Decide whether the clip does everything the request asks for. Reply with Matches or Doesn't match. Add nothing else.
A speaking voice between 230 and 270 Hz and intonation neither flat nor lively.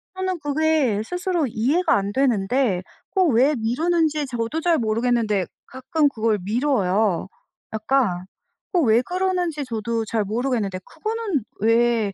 Doesn't match